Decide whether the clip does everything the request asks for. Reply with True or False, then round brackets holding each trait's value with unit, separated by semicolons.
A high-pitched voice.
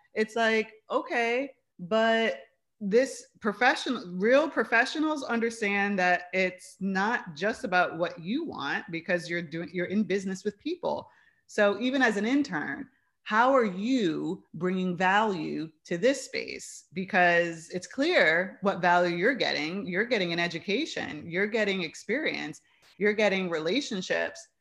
True (205 Hz)